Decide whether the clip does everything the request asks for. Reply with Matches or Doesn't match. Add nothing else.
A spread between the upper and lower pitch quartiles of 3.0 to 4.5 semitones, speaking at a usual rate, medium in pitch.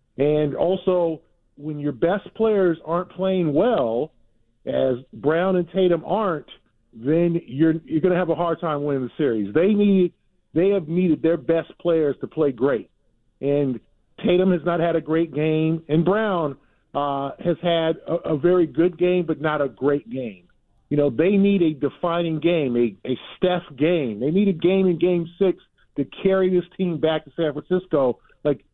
Matches